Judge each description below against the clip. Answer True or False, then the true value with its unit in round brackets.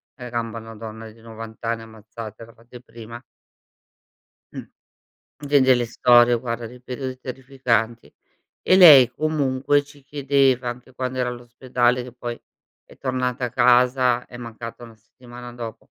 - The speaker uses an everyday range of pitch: False (1.9 semitones)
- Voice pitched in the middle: False (120 Hz)